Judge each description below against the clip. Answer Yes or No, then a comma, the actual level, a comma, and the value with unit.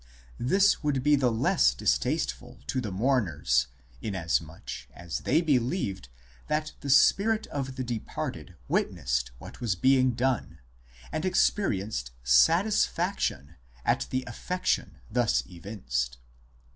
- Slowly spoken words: Yes, slow, 120 wpm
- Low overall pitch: Yes, low, 120 Hz